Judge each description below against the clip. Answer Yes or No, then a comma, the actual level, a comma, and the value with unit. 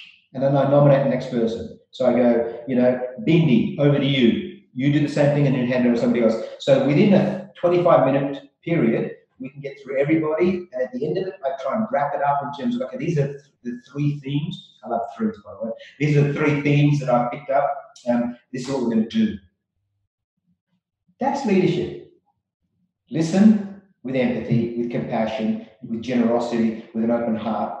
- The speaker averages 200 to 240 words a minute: Yes, fast, 205 wpm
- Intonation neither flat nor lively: No, wide, 6.5 semitones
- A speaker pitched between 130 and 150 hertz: Yes, medium, 140 Hz